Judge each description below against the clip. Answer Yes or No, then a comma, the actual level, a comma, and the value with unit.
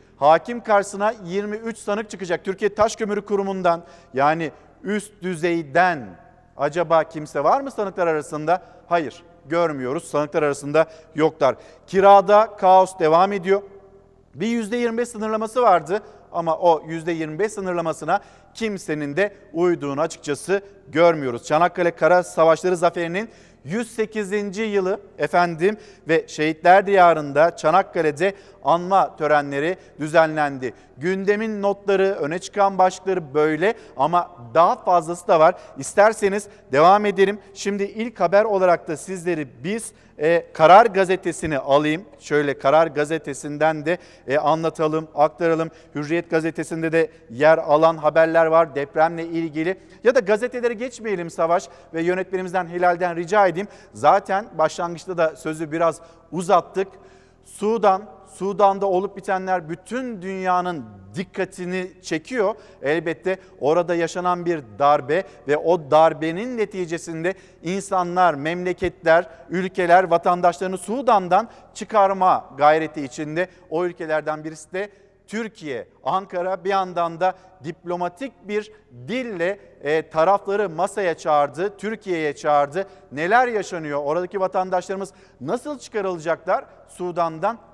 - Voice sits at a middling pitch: Yes, medium, 180 Hz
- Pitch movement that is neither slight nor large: Yes, average, 3.5 semitones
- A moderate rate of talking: Yes, average, 110 wpm